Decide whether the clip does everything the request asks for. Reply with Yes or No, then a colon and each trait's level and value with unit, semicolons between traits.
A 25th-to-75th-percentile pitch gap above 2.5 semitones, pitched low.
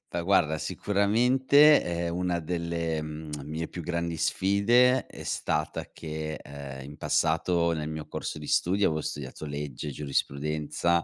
Yes: average, 2.9 semitones; very low, 80 Hz